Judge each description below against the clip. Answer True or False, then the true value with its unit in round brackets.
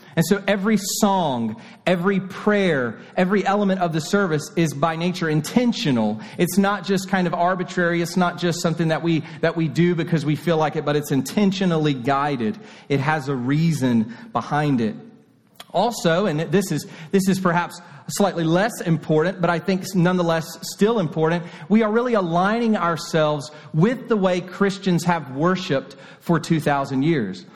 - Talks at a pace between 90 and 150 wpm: False (165 wpm)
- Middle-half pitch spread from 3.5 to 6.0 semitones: True (3.8 semitones)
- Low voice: False (175 Hz)